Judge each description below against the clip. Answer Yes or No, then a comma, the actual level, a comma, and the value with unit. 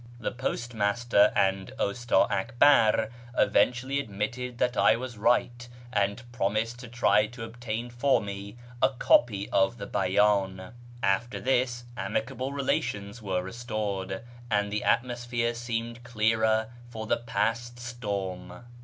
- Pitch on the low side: Yes, low, 115 Hz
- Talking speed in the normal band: No, slow, 125 wpm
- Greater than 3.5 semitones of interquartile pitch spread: No, average, 3.0 semitones